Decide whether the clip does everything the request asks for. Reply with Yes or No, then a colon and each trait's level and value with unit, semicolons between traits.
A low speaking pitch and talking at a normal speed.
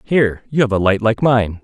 No: low, 115 Hz; fast, 260 wpm